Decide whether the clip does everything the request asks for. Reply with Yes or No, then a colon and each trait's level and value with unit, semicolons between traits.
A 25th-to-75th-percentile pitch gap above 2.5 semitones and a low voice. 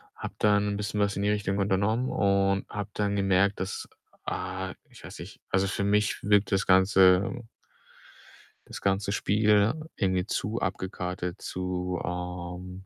No: narrow, 1.8 semitones; low, 100 Hz